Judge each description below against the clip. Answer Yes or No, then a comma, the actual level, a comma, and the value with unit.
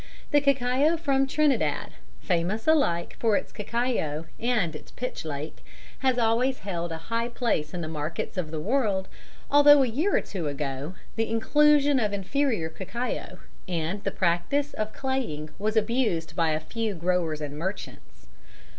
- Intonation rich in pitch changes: Yes, wide, 7.9 semitones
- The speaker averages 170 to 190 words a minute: No, average, 155 wpm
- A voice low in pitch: No, high, 215 Hz